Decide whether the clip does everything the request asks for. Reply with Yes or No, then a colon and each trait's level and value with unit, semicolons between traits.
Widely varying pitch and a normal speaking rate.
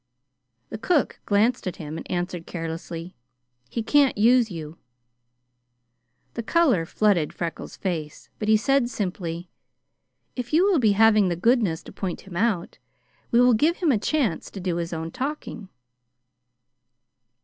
Yes: wide, 6.2 semitones; average, 150 wpm